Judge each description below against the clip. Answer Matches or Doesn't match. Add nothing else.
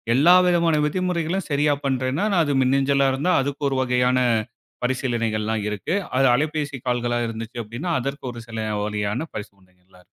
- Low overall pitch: Matches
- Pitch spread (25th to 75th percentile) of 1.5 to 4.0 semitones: Doesn't match